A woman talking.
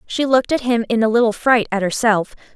Yes: female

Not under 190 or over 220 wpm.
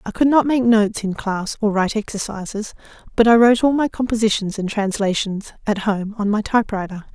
Yes: average, 195 wpm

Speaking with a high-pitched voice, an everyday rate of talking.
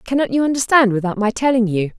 No: high, 235 Hz; fast, 210 wpm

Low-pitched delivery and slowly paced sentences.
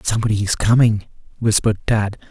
Yes: low, 110 Hz; slow, 130 wpm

